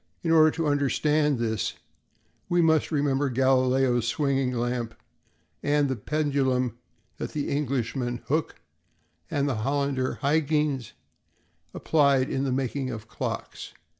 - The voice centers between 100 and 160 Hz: Yes, low, 135 Hz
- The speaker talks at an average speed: No, slow, 120 wpm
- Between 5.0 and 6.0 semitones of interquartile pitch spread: No, narrow, 2.6 semitones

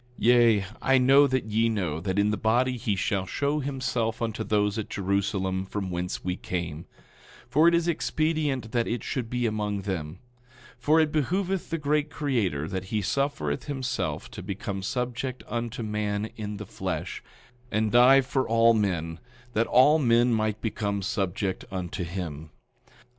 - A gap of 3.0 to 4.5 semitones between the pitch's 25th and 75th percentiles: No, average, 4.9 semitones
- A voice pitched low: Yes, low, 110 Hz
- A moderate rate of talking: Yes, average, 165 wpm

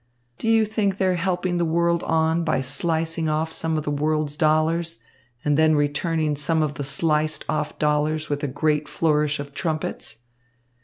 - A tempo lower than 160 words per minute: No, average, 170 wpm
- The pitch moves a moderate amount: No, narrow, 1.9 semitones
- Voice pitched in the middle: Yes, medium, 155 Hz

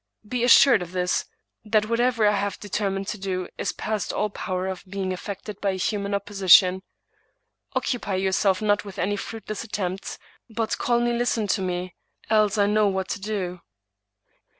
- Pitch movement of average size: No, narrow, 2.2 semitones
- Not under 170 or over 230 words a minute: Yes, average, 175 wpm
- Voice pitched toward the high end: Yes, high, 200 Hz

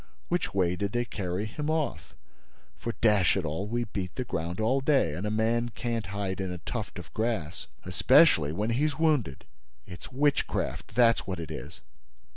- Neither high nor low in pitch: No, low, 110 Hz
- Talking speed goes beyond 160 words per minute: Yes, average, 180 wpm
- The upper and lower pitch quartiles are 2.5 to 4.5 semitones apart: No, average, 5.0 semitones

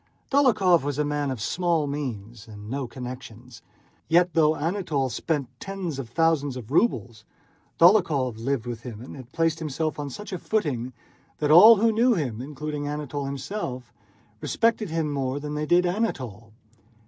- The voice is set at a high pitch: No, medium, 145 Hz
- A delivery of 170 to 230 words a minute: No, average, 160 wpm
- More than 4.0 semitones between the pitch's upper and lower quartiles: Yes, average, 5.0 semitones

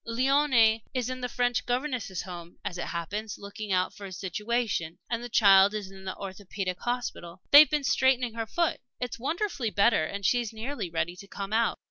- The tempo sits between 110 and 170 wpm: No, average, 190 wpm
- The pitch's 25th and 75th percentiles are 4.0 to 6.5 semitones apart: Yes, average, 4.4 semitones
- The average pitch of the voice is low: No, high, 220 Hz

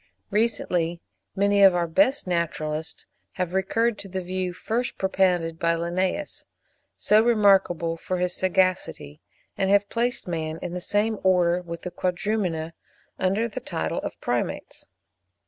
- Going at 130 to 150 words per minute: Yes, average, 145 wpm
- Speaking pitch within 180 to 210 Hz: Yes, medium, 185 Hz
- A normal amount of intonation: Yes, average, 3.0 semitones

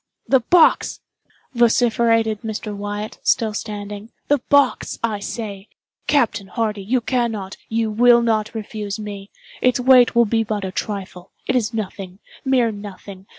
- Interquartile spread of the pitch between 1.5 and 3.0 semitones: Yes, narrow, 2.6 semitones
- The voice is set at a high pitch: Yes, high, 220 Hz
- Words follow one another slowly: Yes, slow, 130 wpm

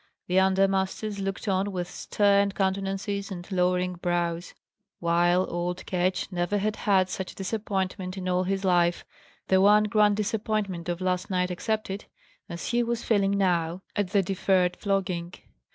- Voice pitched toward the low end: No, high, 190 Hz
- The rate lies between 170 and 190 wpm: No, average, 155 wpm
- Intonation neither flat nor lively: No, narrow, 1.9 semitones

